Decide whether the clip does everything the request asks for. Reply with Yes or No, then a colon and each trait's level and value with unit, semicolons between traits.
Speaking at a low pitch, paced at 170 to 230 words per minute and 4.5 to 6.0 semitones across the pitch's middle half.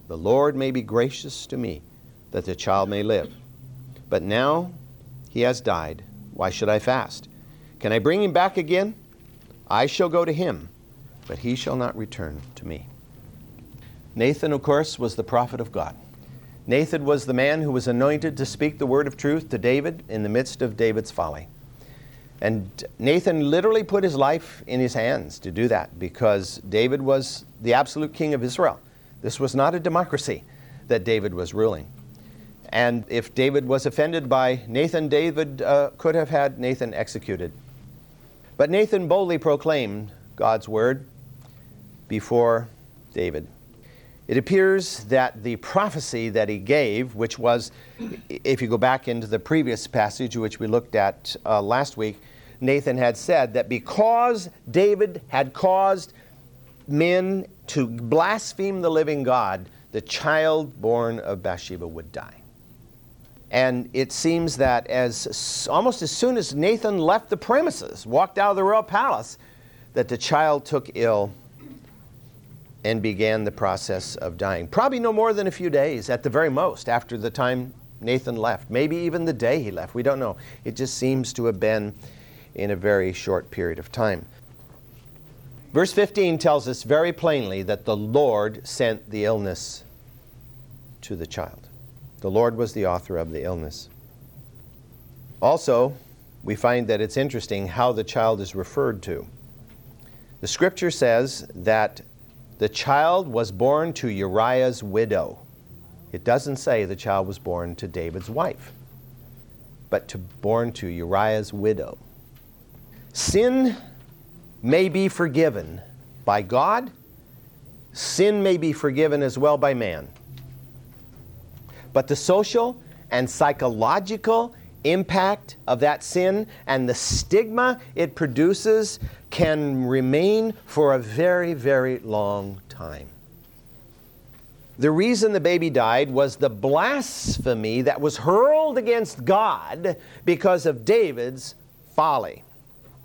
No: low, 130 Hz; average, 145 wpm; average, 4.8 semitones